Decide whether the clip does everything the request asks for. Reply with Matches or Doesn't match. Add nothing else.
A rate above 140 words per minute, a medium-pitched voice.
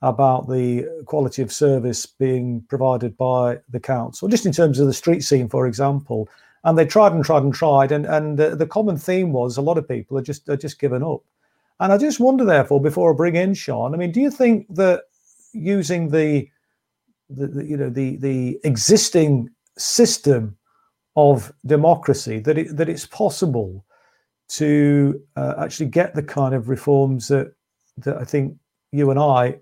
Matches